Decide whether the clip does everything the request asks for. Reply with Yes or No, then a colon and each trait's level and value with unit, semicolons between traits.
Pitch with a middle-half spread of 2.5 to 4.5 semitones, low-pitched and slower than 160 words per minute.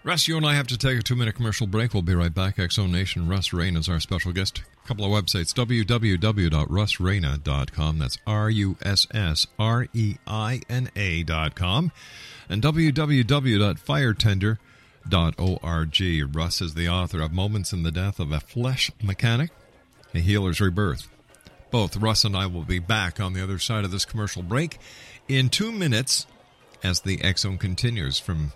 No: average, 4.9 semitones; low, 100 Hz; average, 150 wpm